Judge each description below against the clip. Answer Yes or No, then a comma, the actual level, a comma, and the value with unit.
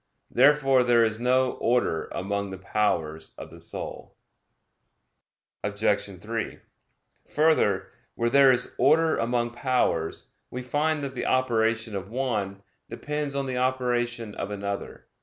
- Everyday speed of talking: No, slow, 130 wpm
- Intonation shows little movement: No, average, 4.2 semitones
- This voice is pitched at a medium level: No, low, 120 Hz